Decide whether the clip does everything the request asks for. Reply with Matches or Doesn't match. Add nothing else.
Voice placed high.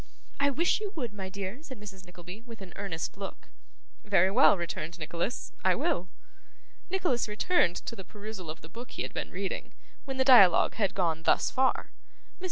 Matches